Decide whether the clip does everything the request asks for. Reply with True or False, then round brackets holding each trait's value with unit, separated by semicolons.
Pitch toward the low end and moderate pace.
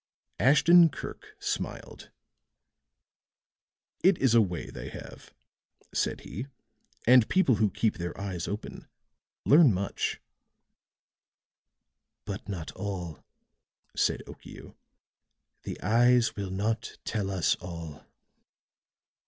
False (105 Hz; 100 wpm)